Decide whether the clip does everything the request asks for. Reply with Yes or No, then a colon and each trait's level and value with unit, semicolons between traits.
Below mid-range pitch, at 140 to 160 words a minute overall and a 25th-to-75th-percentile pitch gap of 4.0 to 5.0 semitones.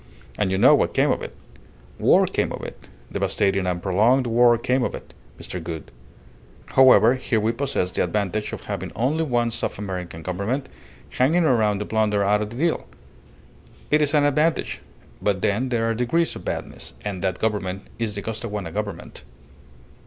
No: low, 110 Hz; average, 175 wpm; average, 4.3 semitones